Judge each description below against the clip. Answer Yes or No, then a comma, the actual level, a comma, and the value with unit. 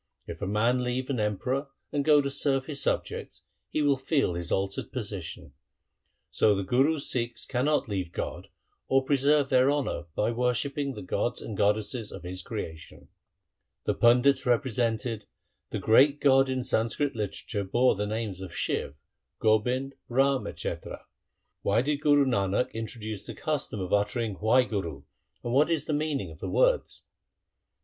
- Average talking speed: Yes, average, 165 wpm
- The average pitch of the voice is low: Yes, low, 125 Hz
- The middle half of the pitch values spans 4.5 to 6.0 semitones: Yes, average, 4.9 semitones